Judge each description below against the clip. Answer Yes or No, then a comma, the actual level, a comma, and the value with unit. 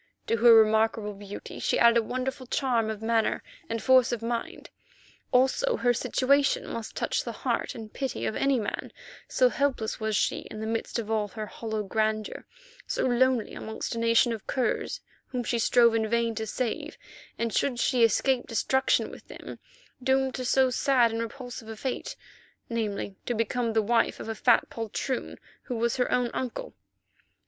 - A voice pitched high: Yes, high, 230 Hz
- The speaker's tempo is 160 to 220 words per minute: Yes, average, 180 wpm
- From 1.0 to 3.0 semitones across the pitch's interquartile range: Yes, narrow, 2.5 semitones